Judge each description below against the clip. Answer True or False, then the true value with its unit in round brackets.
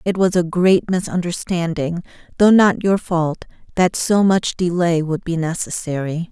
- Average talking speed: True (150 wpm)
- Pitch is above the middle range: False (175 Hz)